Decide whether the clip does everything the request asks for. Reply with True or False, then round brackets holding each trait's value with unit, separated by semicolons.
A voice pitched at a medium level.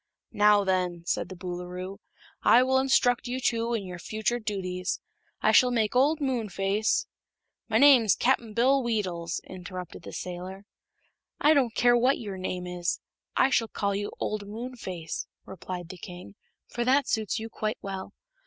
False (210 Hz)